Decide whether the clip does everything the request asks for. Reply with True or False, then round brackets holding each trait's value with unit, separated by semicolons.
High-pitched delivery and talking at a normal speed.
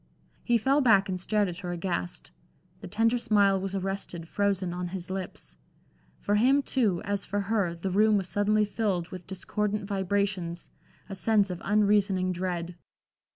True (195 Hz; 160 wpm)